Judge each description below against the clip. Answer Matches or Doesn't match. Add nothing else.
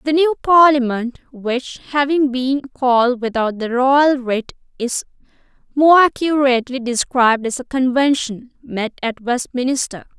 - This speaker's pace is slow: Matches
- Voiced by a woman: Matches